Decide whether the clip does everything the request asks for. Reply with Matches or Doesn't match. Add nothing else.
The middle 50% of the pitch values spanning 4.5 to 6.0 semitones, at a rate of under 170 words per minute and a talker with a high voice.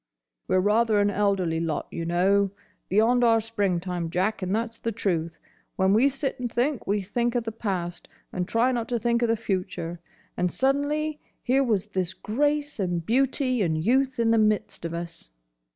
Doesn't match